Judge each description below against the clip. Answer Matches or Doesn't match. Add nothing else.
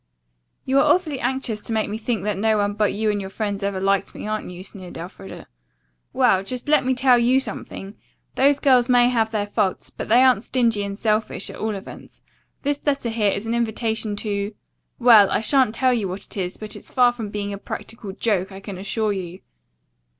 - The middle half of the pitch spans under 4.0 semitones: Matches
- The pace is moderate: Doesn't match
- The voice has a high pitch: Matches